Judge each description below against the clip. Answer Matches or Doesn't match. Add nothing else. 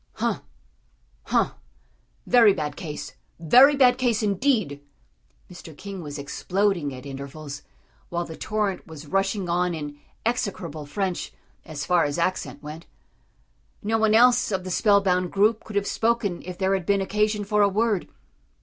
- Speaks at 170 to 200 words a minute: Doesn't match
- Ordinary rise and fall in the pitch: Matches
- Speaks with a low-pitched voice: Doesn't match